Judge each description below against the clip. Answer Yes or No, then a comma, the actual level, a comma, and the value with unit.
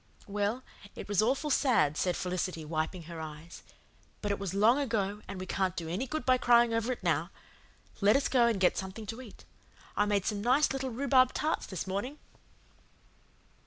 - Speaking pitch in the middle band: No, high, 205 Hz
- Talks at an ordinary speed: Yes, average, 190 wpm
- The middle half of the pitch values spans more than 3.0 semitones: Yes, average, 5.2 semitones